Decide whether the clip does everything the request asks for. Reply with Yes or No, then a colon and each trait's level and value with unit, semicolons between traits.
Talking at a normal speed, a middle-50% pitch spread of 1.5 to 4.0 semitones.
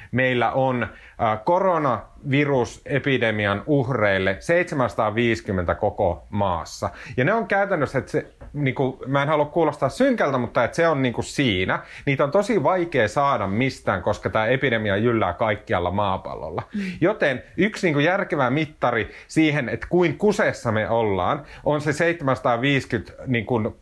No: average, 140 wpm; wide, 5.4 semitones